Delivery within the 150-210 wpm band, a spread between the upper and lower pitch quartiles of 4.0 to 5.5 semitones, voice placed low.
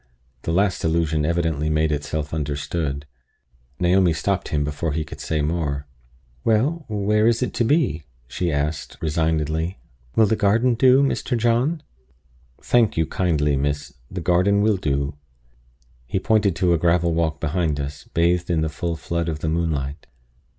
Yes: average, 155 wpm; average, 4.7 semitones; very low, 85 Hz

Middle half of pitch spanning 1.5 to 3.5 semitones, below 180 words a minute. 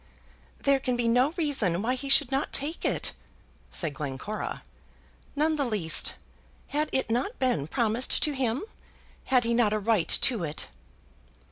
No: average, 4.4 semitones; average, 155 wpm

